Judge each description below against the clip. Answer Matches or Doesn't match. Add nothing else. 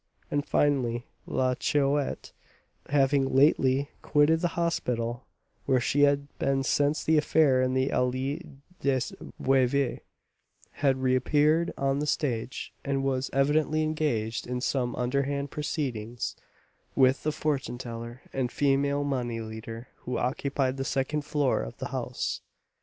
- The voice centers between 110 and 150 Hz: Matches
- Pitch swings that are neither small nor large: Doesn't match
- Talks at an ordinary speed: Doesn't match